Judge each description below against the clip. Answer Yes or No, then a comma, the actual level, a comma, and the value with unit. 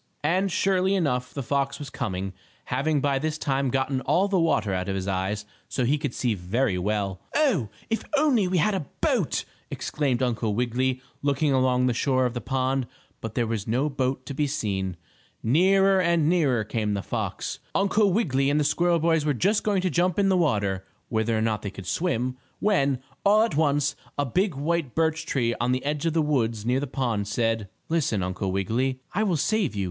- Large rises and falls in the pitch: Yes, wide, 6.3 semitones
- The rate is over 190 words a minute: Yes, fast, 205 wpm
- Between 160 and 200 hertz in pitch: No, low, 135 Hz